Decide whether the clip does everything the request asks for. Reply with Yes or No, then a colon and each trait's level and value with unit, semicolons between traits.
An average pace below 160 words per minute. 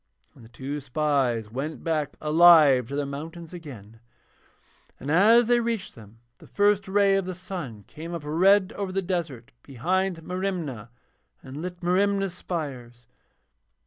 Yes: average, 145 wpm